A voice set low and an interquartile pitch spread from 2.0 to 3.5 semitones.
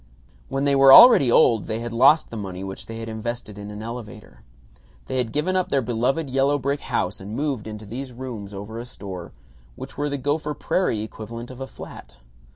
No: low, 120 Hz; average, 4.3 semitones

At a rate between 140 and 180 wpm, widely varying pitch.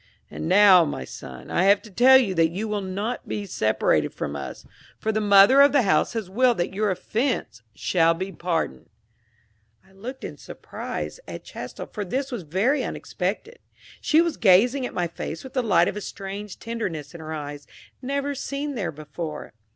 No: average, 190 wpm; wide, 6.4 semitones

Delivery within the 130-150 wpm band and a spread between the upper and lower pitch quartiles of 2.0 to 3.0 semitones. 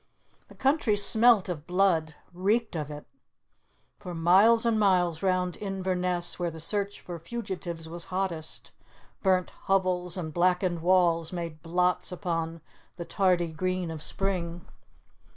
Yes: slow, 135 wpm; narrow, 2.4 semitones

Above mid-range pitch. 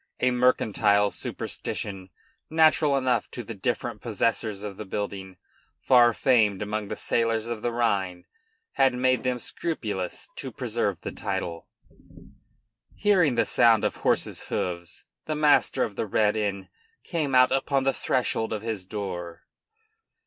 No: low, 115 Hz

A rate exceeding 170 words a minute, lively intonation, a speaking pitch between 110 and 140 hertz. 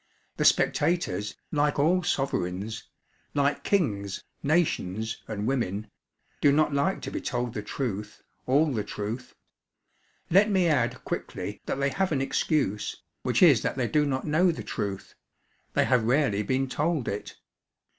No: average, 150 wpm; wide, 6.2 semitones; low, 135 Hz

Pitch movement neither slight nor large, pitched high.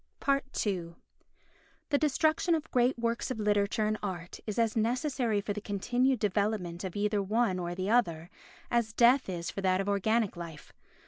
Yes: average, 4.0 semitones; high, 210 Hz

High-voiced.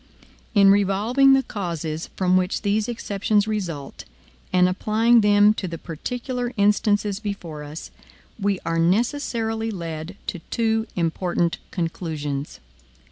Yes: high, 200 Hz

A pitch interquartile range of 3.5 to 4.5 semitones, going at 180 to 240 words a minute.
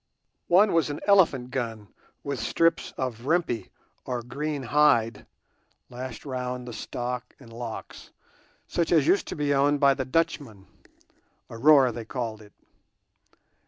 No: average, 4.0 semitones; slow, 135 wpm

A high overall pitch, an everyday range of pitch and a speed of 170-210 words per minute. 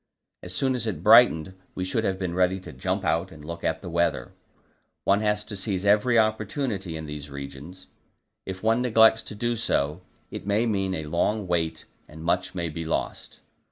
No: very low, 95 Hz; average, 4.5 semitones; average, 195 wpm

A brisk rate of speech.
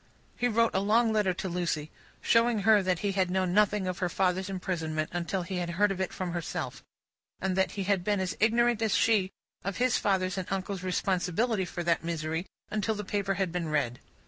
Yes: fast, 210 wpm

